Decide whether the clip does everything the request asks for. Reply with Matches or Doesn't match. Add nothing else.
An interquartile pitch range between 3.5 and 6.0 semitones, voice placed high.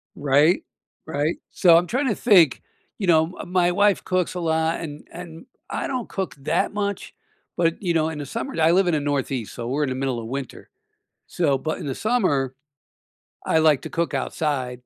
Doesn't match